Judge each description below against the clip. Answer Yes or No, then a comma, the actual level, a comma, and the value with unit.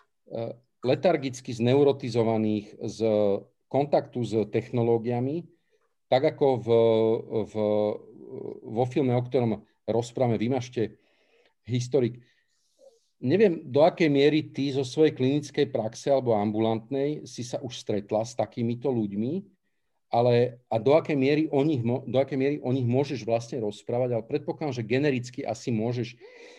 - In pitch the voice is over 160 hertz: No, low, 125 Hz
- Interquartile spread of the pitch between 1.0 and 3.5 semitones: No, average, 4.0 semitones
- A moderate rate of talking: Yes, average, 125 wpm